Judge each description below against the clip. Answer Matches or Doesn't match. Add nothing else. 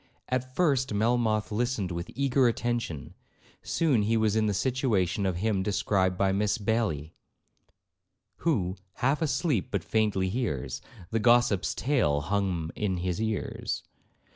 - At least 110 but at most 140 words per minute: Matches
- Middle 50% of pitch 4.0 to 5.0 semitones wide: Matches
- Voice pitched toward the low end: Matches